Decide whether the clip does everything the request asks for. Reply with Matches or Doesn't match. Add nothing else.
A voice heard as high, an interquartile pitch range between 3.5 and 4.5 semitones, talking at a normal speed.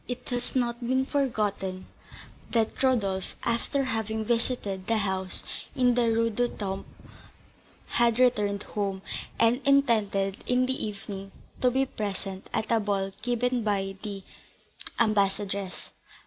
Doesn't match